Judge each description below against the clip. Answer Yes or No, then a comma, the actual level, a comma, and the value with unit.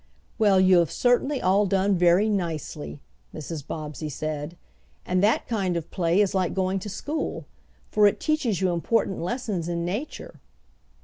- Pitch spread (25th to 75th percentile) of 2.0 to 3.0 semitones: No, average, 3.5 semitones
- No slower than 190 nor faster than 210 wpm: No, average, 160 wpm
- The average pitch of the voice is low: No, medium, 185 Hz